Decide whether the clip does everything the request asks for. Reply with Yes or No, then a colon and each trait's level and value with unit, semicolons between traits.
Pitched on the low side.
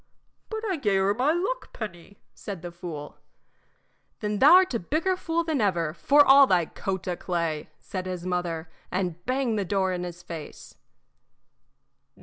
No: high, 190 Hz